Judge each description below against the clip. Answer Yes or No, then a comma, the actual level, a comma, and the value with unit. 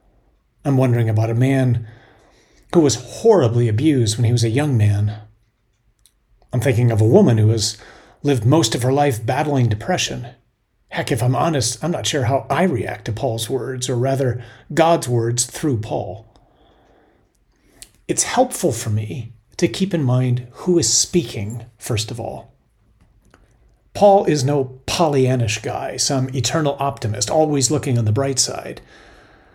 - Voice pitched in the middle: No, low, 125 Hz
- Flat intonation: No, average, 3.8 semitones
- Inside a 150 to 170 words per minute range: Yes, average, 155 wpm